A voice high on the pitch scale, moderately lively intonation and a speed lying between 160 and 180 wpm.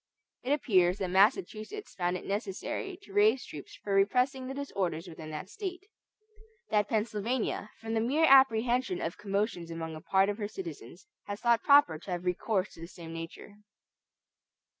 No: high, 210 Hz; wide, 6.2 semitones; average, 165 wpm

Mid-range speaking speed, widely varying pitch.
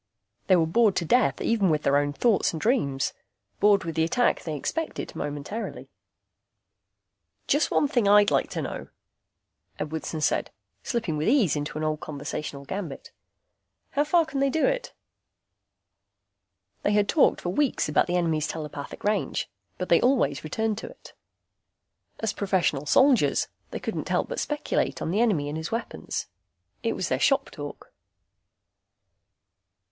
Yes: average, 155 wpm; wide, 7.6 semitones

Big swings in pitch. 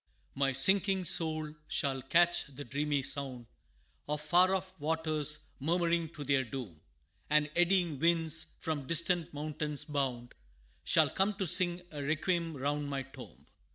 No: average, 3.5 semitones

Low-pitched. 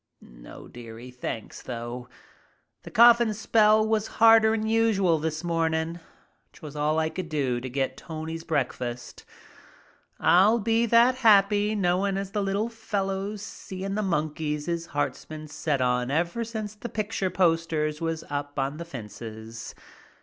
No: medium, 170 Hz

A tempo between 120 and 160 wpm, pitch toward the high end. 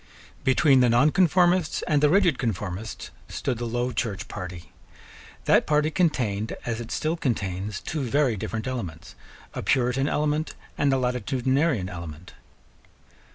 No: slow, 135 wpm; low, 125 Hz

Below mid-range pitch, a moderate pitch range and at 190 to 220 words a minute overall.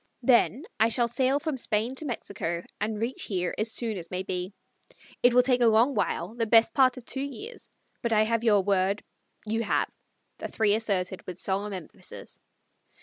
No: high, 225 Hz; average, 3.7 semitones; average, 195 wpm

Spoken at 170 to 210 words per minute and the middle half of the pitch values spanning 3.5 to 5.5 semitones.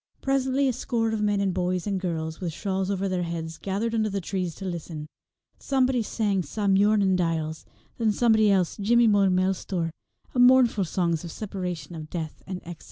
Yes: average, 190 wpm; average, 3.9 semitones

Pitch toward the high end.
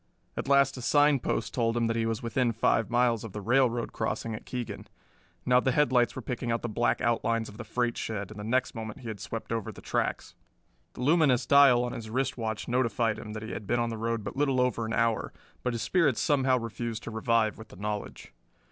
No: low, 115 Hz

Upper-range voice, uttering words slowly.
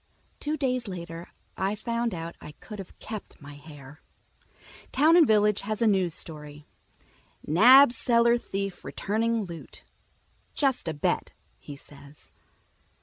Yes: high, 200 Hz; slow, 130 wpm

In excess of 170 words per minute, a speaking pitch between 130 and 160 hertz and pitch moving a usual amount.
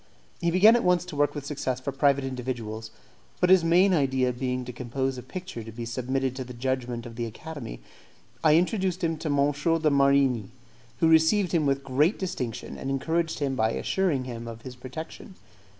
Yes: average, 195 wpm; low, 135 Hz; average, 4.5 semitones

